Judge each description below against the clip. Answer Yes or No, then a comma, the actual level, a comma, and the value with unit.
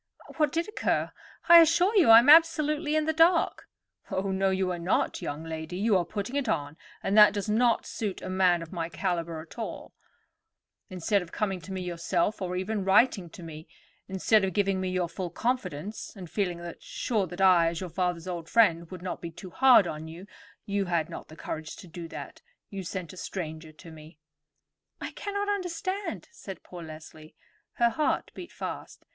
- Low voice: No, high, 190 Hz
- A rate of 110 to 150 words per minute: No, average, 190 wpm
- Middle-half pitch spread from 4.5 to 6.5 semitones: Yes, average, 5.1 semitones